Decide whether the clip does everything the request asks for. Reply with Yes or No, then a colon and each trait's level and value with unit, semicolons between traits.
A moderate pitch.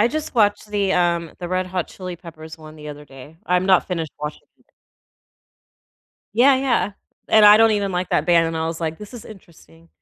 Yes: medium, 180 Hz